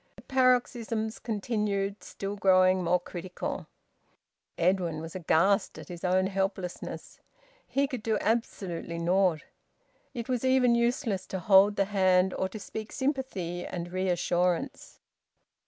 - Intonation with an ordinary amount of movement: Yes, average, 3.6 semitones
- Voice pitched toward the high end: Yes, high, 195 Hz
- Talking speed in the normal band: No, slow, 125 wpm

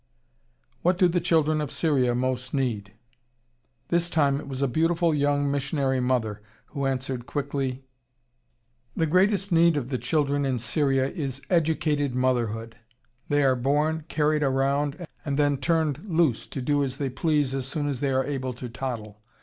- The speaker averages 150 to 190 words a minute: Yes, average, 165 wpm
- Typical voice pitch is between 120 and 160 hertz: Yes, medium, 140 Hz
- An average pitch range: Yes, average, 3.1 semitones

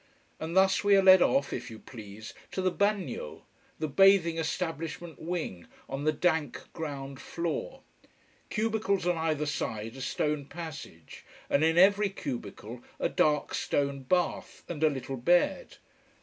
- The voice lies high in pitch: No, medium, 160 Hz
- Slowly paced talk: No, average, 150 wpm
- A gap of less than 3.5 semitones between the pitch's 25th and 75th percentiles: No, average, 5.1 semitones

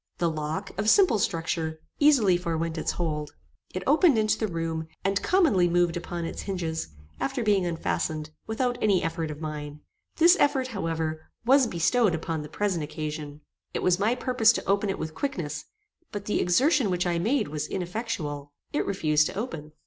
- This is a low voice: No, medium, 175 Hz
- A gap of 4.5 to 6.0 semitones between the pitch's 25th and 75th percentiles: Yes, wide, 5.6 semitones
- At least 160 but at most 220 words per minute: Yes, average, 175 wpm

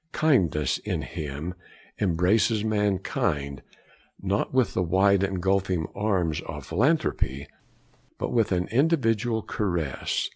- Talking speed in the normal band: No, slow, 105 wpm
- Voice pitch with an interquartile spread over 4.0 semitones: Yes, average, 4.6 semitones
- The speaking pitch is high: No, very low, 95 Hz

